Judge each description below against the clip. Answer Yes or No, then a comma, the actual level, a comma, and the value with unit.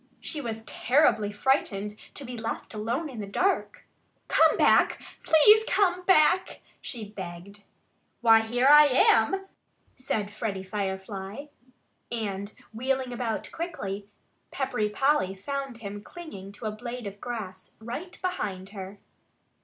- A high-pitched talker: Yes, high, 225 Hz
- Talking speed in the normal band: No, slow, 130 wpm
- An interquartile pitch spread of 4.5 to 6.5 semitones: Yes, wide, 5.4 semitones